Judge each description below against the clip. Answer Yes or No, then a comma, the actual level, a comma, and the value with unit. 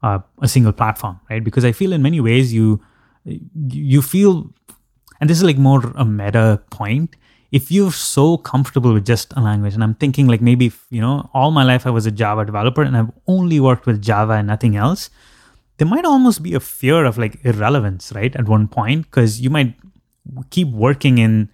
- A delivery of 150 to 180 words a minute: No, fast, 205 wpm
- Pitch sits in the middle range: No, low, 125 Hz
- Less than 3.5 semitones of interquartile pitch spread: No, average, 4.3 semitones